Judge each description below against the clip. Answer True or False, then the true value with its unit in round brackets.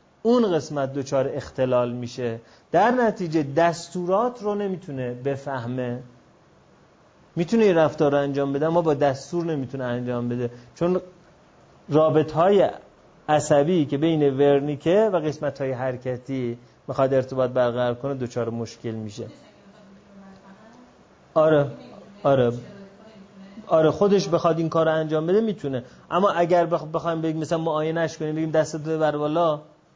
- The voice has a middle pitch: True (155 Hz)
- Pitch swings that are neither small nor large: True (4.6 semitones)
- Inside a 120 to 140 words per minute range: True (125 wpm)